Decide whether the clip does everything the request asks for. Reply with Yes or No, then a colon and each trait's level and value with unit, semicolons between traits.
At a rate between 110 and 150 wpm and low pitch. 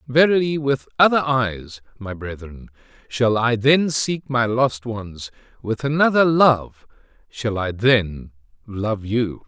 Yes: slow, 135 wpm; low, 120 Hz